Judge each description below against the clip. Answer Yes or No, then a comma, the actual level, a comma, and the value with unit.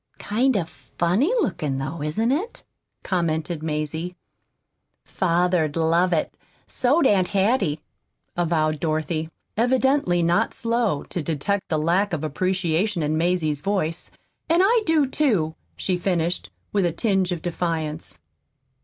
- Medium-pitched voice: Yes, medium, 175 Hz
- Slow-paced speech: Yes, slow, 125 wpm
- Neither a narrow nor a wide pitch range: Yes, average, 4.5 semitones